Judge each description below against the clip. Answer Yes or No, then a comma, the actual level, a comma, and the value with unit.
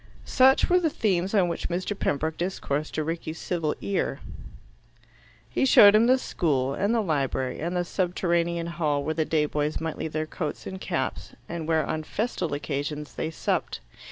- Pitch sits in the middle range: Yes, medium, 165 Hz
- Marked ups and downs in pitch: No, average, 3.6 semitones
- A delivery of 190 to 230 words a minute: No, average, 180 wpm